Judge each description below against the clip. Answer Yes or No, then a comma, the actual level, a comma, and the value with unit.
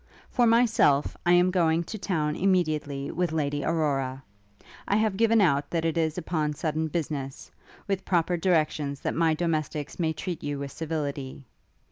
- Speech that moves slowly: No, average, 160 wpm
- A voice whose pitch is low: No, medium, 160 Hz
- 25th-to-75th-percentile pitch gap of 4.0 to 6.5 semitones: No, average, 3.4 semitones